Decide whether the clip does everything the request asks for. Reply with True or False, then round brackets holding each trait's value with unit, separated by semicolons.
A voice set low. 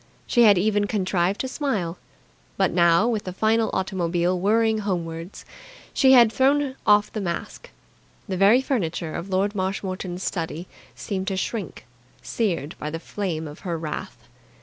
False (190 Hz)